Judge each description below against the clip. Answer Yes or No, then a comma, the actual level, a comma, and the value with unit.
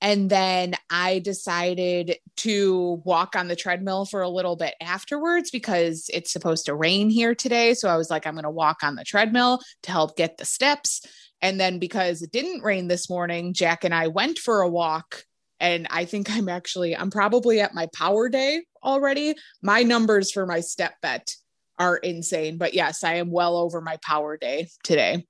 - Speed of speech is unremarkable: Yes, average, 195 wpm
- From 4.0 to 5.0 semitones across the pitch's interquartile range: No, average, 3.5 semitones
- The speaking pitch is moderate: Yes, medium, 180 Hz